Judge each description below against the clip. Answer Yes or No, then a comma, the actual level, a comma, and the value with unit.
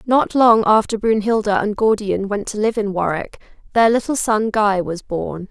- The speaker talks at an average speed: Yes, average, 185 wpm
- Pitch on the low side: No, high, 210 Hz